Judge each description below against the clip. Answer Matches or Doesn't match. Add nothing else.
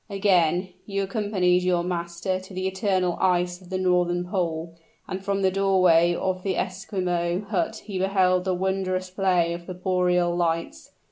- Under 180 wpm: Matches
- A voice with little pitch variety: Matches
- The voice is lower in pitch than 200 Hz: Matches